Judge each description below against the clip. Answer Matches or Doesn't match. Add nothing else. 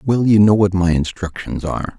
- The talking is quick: Matches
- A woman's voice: Doesn't match